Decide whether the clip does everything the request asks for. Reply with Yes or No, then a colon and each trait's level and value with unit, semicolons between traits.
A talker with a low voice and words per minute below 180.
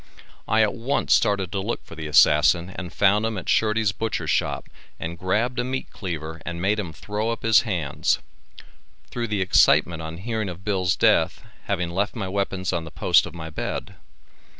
No: very low, 95 Hz; average, 190 wpm